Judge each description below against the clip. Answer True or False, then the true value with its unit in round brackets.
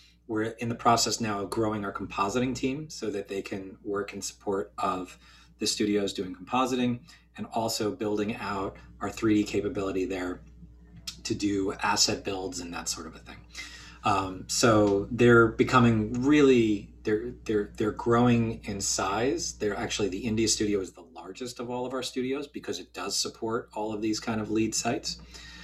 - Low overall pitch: True (110 Hz)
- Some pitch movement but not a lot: True (3.1 semitones)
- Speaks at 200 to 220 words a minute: False (175 wpm)